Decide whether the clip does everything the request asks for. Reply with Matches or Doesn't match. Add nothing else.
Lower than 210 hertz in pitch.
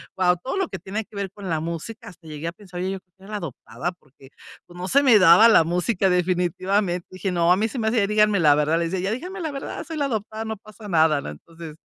Matches